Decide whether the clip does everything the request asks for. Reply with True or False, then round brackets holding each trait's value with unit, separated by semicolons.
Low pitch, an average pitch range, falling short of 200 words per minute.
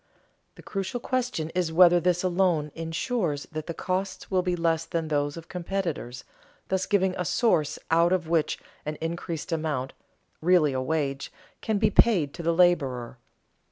False (170 Hz; 3.1 semitones; 160 wpm)